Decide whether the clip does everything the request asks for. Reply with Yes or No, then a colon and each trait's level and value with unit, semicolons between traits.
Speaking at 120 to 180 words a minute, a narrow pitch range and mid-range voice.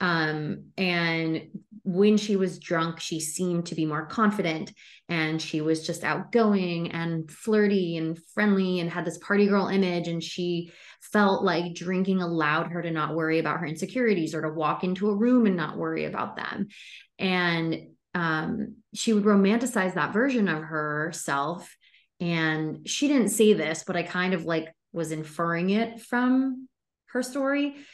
No: average, 165 wpm; average, 4.2 semitones; medium, 175 Hz